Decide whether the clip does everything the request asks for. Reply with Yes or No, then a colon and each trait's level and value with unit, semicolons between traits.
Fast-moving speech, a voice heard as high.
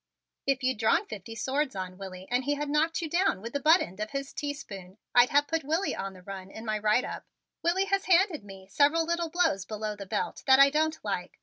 Yes: fast, 235 wpm; very high, 270 Hz